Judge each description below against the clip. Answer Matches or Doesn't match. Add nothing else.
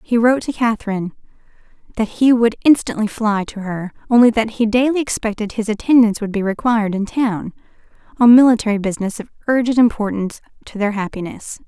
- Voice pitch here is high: Matches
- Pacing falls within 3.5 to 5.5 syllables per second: Doesn't match